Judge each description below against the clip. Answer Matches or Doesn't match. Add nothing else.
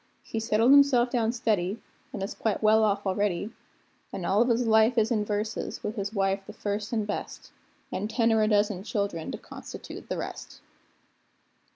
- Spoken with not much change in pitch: Matches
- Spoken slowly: Doesn't match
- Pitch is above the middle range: Matches